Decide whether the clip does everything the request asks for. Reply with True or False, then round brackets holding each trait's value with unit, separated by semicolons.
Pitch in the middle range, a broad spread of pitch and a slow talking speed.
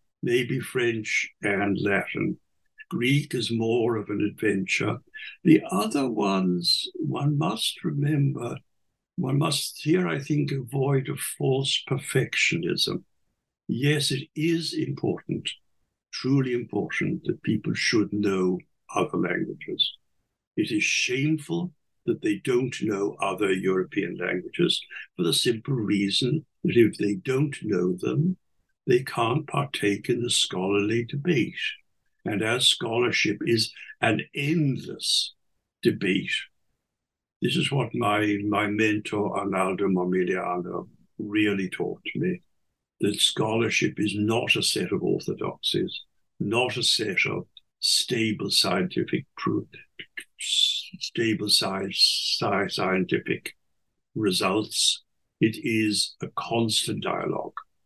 False (120 Hz; 6.0 semitones; 110 wpm)